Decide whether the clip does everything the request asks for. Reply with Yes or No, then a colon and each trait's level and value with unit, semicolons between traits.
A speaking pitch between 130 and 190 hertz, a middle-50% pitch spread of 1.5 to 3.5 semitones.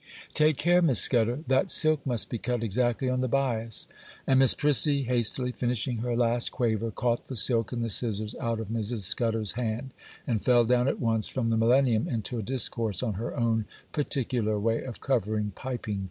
No: low, 120 Hz; narrow, 2.4 semitones